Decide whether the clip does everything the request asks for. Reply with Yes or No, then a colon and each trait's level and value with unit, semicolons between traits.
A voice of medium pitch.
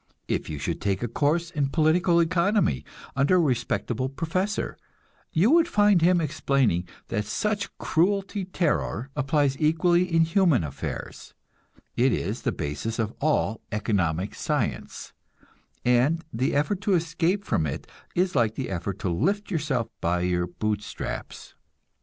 Yes: medium, 145 Hz